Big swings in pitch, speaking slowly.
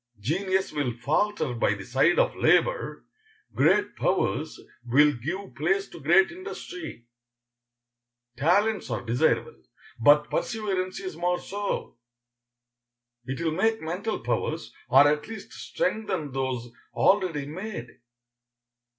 Yes: wide, 6.8 semitones; slow, 115 wpm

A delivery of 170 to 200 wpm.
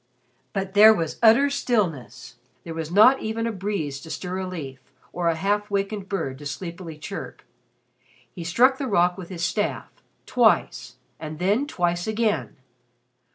No: average, 155 wpm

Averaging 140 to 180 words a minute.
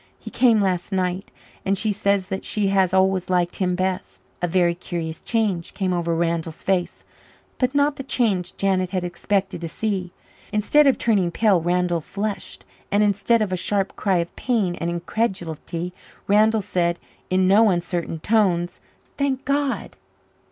Yes: average, 160 wpm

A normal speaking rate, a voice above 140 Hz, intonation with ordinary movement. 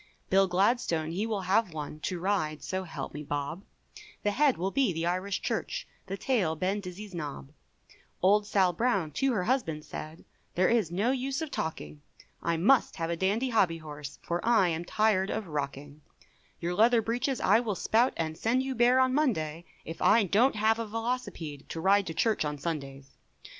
No: average, 190 wpm; high, 190 Hz; wide, 5.9 semitones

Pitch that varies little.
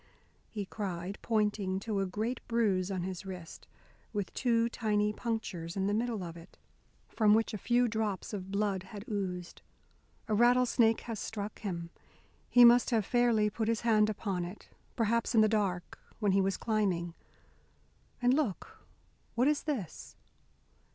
No: average, 3.3 semitones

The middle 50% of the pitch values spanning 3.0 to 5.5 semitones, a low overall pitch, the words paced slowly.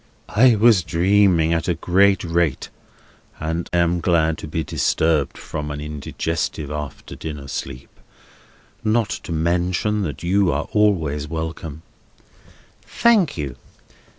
Yes: average, 3.8 semitones; very low, 85 Hz; slow, 125 wpm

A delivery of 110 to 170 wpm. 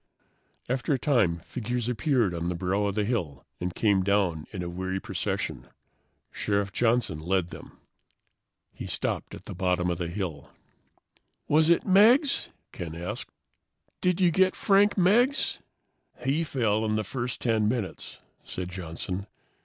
Yes: average, 150 wpm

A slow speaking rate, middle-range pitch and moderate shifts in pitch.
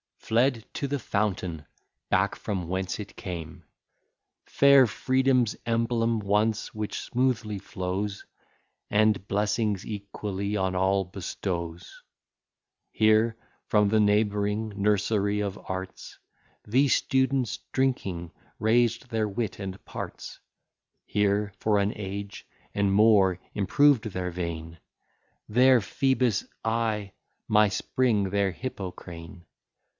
No: slow, 105 wpm; low, 105 Hz; average, 3.0 semitones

